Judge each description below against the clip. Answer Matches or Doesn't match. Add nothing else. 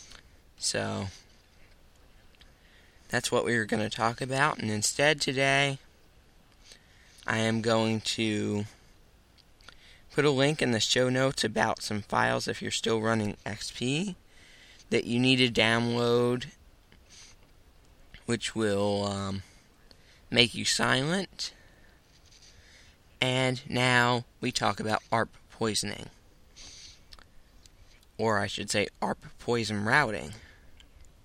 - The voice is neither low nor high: Doesn't match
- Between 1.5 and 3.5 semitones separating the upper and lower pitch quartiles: Doesn't match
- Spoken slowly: Matches